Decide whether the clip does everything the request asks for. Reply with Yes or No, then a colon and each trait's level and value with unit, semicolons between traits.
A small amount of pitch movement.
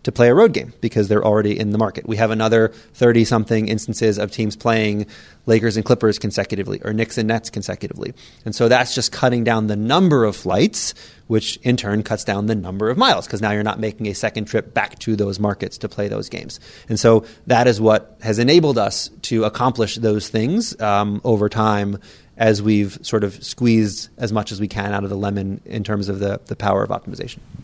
Yes: narrow, 1.6 semitones